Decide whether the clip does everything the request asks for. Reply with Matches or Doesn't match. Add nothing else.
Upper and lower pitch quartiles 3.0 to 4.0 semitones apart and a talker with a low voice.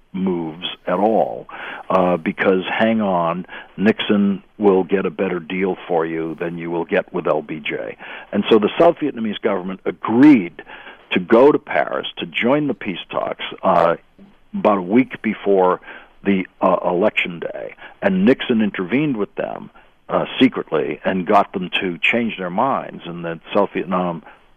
Matches